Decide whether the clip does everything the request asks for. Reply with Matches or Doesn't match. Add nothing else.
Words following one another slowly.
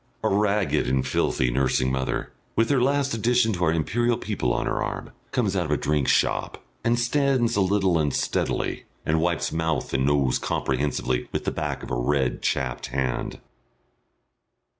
Doesn't match